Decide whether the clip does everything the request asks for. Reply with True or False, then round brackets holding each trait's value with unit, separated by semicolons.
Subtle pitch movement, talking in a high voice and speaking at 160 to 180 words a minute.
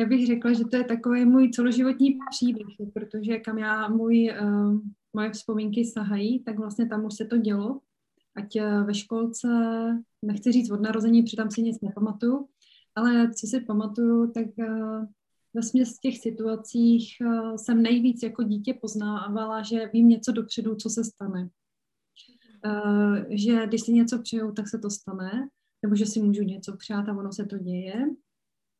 True (1.8 semitones; 225 Hz; 170 wpm)